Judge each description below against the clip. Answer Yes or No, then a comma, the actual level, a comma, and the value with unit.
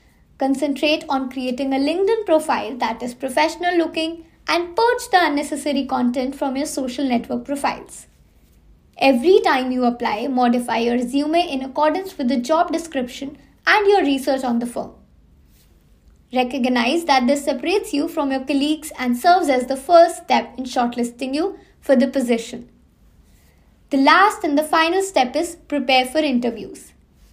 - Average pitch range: Yes, average, 4.0 semitones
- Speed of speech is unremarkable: Yes, average, 150 wpm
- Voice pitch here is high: Yes, very high, 280 Hz